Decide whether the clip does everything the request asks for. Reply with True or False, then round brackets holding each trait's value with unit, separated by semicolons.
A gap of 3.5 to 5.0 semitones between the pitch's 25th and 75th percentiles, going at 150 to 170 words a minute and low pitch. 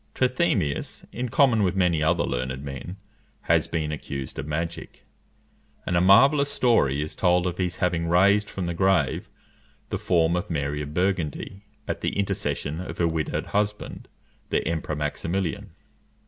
True (4.3 semitones; 155 wpm; 85 Hz)